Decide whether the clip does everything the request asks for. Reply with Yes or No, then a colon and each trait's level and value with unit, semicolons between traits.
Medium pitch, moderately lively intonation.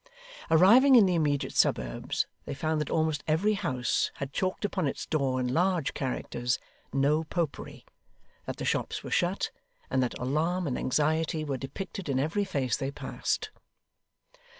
Yes: medium, 155 Hz; average, 4.7 semitones